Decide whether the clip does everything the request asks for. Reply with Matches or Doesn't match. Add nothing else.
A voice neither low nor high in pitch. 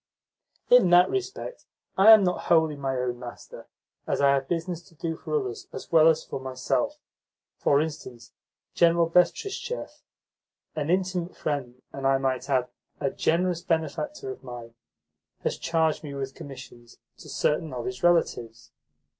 Matches